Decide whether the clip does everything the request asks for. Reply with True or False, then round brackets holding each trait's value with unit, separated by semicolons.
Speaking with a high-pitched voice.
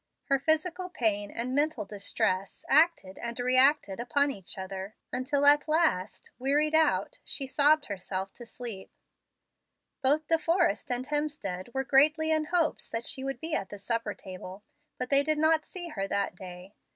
True (265 Hz)